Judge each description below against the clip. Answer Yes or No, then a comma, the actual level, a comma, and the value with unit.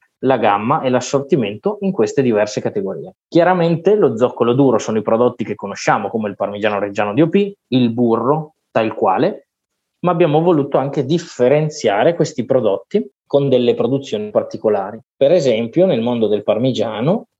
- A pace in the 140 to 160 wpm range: Yes, average, 150 wpm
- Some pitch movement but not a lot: No, wide, 6.0 semitones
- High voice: No, low, 135 Hz